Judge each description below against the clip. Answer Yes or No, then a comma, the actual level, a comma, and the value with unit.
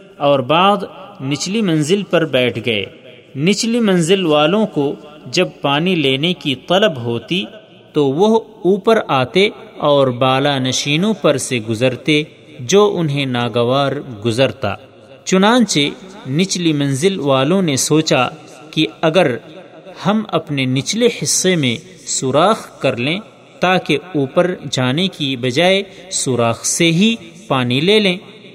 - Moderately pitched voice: Yes, medium, 155 Hz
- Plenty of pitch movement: Yes, wide, 6.0 semitones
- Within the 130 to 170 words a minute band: No, average, 120 wpm